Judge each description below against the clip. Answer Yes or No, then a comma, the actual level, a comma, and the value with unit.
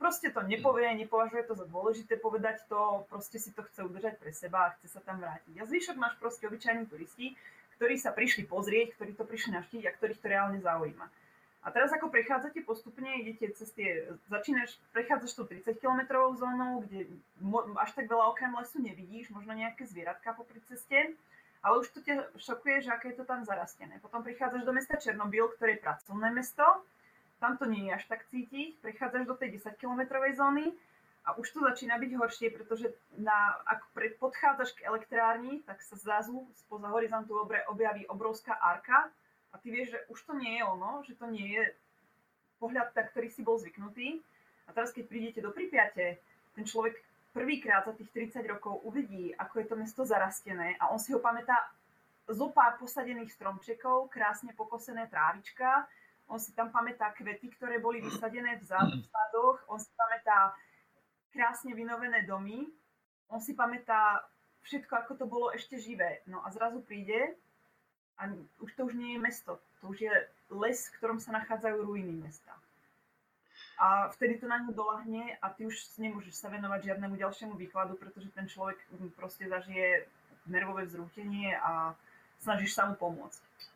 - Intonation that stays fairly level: No, average, 3.2 semitones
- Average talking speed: No, fast, 175 wpm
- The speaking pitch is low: No, high, 225 Hz